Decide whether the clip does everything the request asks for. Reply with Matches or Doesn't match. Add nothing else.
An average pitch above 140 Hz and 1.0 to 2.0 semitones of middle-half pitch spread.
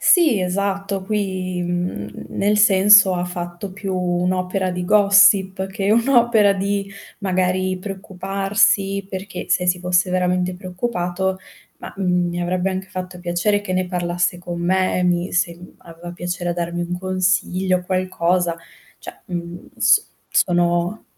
Matches